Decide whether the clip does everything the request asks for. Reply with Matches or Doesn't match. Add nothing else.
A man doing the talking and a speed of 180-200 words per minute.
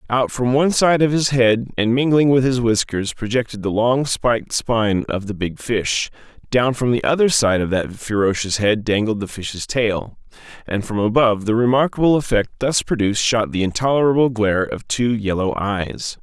Matches